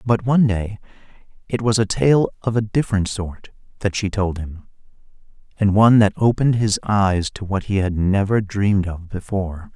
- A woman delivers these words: No, male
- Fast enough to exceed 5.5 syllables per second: No, 5.2 syllables/s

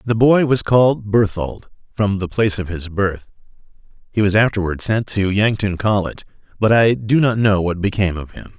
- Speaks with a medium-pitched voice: No, low, 105 Hz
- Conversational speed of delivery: Yes, average, 190 wpm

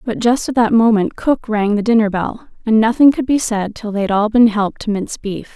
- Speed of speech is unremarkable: No, fast, 260 wpm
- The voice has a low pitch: No, high, 220 Hz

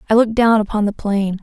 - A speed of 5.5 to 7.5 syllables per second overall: Yes, 6.6 syllables/s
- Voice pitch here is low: No, high, 215 Hz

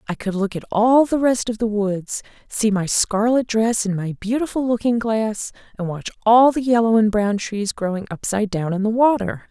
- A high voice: Yes, high, 220 Hz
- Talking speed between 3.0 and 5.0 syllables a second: Yes, 4.9 syllables/s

